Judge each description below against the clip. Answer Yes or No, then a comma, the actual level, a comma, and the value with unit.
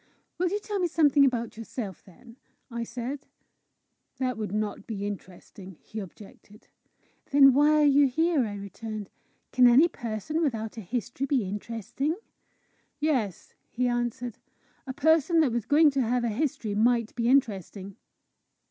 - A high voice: Yes, high, 240 Hz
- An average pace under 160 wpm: Yes, average, 150 wpm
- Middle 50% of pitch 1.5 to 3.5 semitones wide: No, average, 4.8 semitones